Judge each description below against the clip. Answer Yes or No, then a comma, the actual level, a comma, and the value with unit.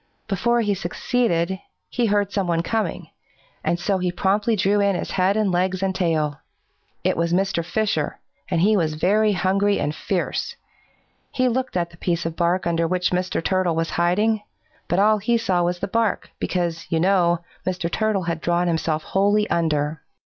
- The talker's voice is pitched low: No, medium, 185 Hz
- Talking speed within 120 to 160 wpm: No, average, 175 wpm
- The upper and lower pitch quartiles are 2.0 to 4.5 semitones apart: Yes, average, 3.2 semitones